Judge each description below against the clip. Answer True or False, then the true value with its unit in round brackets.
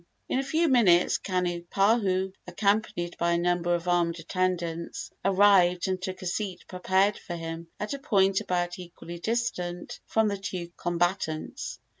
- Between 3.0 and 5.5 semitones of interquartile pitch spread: False (2.4 semitones)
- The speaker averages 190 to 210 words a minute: False (150 wpm)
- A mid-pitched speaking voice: True (180 Hz)